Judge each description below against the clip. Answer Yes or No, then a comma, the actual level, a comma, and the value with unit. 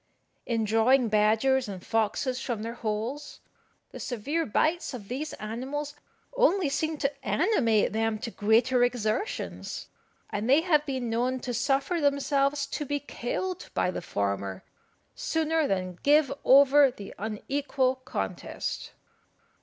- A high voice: Yes, very high, 255 Hz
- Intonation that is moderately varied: Yes, average, 4.7 semitones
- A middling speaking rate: No, slow, 130 wpm